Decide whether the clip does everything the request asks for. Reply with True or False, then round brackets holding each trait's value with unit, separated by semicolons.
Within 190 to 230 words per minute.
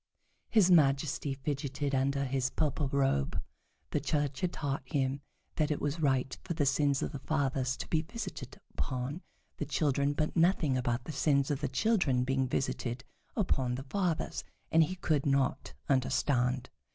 False (165 wpm)